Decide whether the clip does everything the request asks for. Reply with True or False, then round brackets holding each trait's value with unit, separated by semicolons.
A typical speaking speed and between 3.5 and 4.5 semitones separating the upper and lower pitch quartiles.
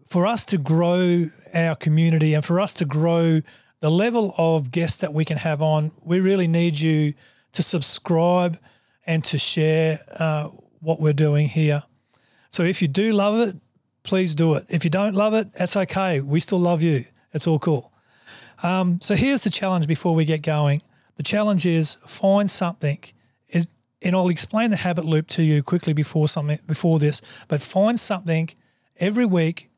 False (180 wpm; 2.9 semitones)